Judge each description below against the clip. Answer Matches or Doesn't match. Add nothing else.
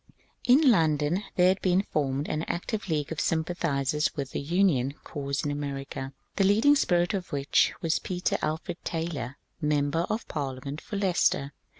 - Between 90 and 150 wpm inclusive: Doesn't match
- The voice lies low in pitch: Doesn't match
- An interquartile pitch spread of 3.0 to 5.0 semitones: Matches